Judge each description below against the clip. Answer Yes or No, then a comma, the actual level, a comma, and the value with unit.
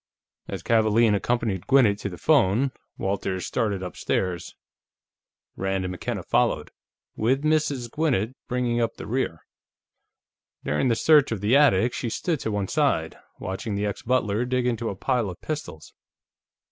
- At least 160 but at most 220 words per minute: No, average, 150 wpm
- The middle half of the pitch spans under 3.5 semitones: No, average, 4.6 semitones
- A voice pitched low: Yes, low, 115 Hz